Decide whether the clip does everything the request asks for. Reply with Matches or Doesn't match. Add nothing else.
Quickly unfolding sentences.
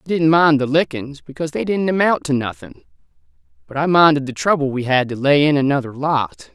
Matches